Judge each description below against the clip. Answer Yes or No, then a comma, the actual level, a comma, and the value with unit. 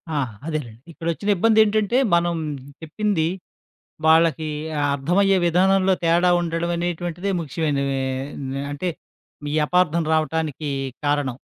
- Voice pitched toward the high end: No, medium, 165 Hz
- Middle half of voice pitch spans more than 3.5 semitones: No, average, 3.1 semitones